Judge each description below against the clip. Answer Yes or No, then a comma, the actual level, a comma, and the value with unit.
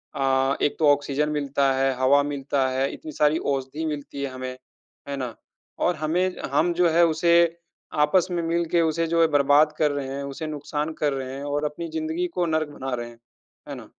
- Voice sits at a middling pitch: Yes, medium, 145 Hz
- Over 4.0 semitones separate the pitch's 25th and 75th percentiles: No, average, 2.8 semitones